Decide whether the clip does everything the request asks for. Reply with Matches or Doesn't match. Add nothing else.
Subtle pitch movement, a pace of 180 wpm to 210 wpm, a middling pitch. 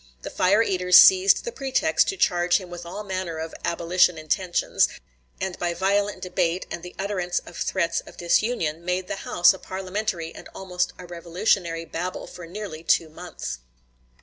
Doesn't match